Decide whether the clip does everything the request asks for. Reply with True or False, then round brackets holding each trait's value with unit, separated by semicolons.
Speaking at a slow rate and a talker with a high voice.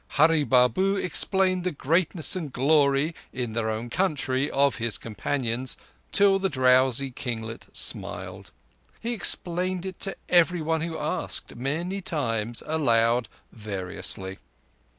False (110 wpm; 140 Hz)